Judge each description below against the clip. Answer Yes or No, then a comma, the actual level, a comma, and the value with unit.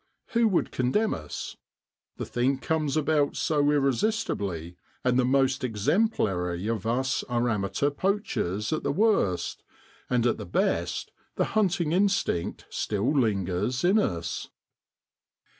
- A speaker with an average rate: No, slow, 125 wpm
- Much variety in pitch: Yes, wide, 7.6 semitones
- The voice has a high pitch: No, low, 130 Hz